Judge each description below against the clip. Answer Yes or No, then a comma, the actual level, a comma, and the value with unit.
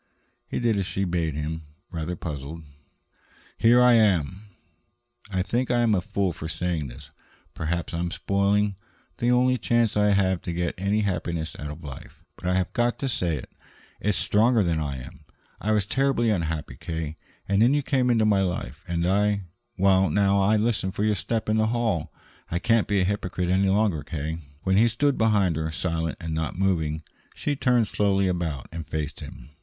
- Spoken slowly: No, average, 190 wpm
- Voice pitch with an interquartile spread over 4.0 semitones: Yes, average, 4.7 semitones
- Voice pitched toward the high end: No, very low, 95 Hz